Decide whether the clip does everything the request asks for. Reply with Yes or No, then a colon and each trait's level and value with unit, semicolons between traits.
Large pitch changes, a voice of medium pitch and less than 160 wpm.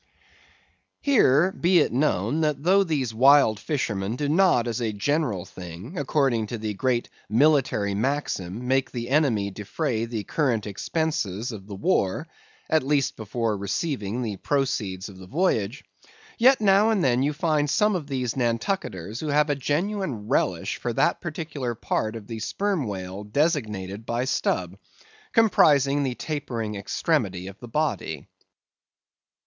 No: wide, 6.2 semitones; low, 125 Hz; average, 150 wpm